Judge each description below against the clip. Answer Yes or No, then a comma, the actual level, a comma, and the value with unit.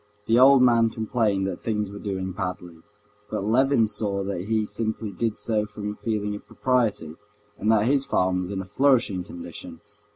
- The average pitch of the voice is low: Yes, low, 105 Hz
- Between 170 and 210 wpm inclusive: Yes, average, 185 wpm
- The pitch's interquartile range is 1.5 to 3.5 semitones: Yes, average, 3.0 semitones